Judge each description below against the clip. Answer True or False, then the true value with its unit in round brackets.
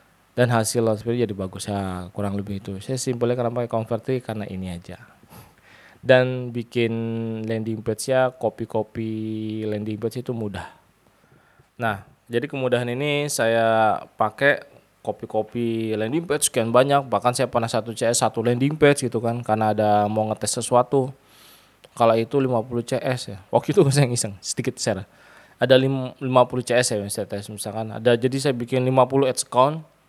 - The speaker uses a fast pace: True (160 wpm)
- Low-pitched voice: True (115 Hz)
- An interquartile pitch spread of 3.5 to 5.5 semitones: False (2.8 semitones)